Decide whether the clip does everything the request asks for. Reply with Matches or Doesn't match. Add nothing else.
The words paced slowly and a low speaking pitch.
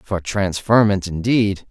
Matches